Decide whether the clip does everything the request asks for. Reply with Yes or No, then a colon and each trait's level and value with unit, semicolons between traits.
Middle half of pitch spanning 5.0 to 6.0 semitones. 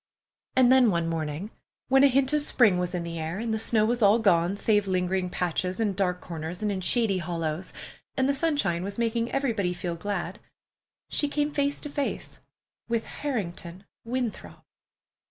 Yes: wide, 5.5 semitones